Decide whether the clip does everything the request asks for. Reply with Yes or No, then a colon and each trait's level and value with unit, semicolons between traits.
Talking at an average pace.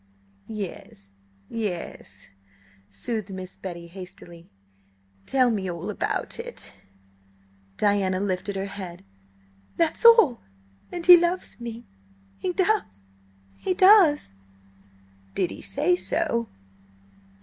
No: slow, 95 wpm